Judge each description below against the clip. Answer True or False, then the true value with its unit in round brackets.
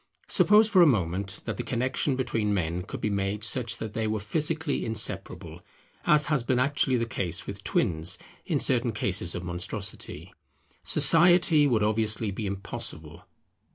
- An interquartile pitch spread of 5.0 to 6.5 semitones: True (5.3 semitones)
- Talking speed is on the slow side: False (155 wpm)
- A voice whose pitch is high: False (110 Hz)